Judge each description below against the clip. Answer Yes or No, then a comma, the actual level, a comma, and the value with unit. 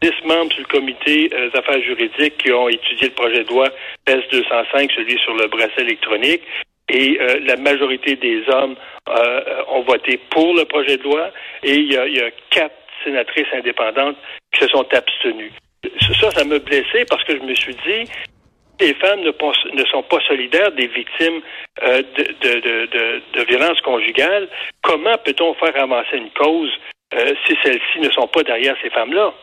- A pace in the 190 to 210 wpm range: No, average, 180 wpm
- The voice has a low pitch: No, medium, 165 Hz